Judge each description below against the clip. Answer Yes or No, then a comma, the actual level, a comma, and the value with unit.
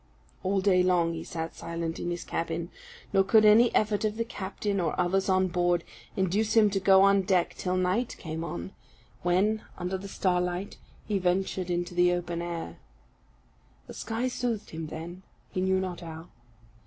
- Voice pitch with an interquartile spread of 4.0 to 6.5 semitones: No, narrow, 2.4 semitones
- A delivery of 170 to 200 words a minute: Yes, average, 175 wpm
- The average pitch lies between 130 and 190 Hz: Yes, medium, 185 Hz